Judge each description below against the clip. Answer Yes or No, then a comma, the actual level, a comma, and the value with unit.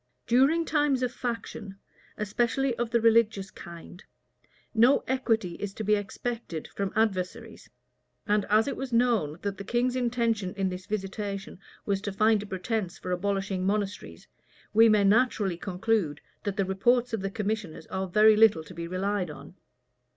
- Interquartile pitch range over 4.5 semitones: No, average, 3.2 semitones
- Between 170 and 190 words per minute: No, average, 160 wpm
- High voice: Yes, high, 210 Hz